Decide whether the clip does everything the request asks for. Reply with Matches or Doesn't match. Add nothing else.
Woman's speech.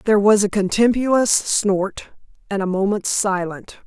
Matches